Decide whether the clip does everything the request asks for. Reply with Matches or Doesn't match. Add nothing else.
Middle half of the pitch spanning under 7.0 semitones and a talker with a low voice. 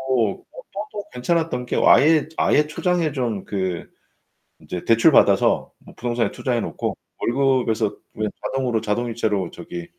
Matches